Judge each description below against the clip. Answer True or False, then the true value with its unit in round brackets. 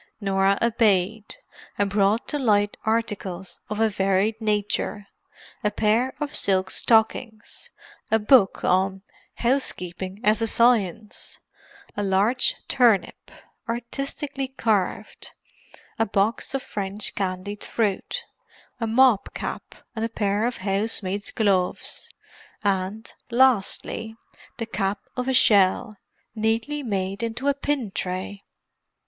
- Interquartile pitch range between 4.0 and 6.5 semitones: False (2.9 semitones)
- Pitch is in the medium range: False (215 Hz)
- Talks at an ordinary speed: False (115 wpm)